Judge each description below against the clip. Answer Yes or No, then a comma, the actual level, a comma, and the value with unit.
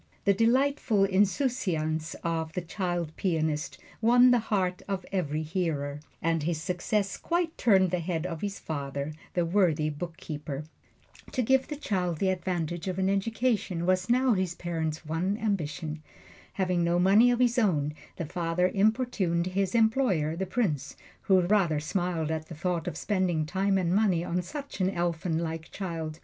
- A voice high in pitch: No, medium, 180 Hz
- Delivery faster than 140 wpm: Yes, average, 160 wpm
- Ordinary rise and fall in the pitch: Yes, average, 3.7 semitones